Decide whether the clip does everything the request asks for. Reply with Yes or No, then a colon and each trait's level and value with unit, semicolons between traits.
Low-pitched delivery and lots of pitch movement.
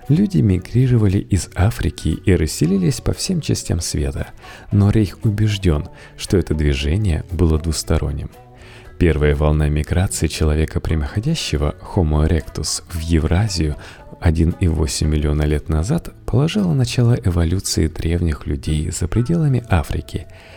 Yes: very low, 90 Hz; wide, 5.8 semitones